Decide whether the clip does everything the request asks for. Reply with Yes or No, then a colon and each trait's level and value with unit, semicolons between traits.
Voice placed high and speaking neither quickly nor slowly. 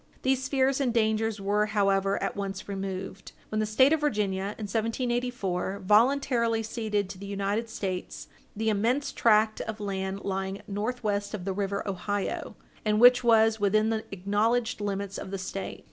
Yes: high, 210 Hz; average, 160 wpm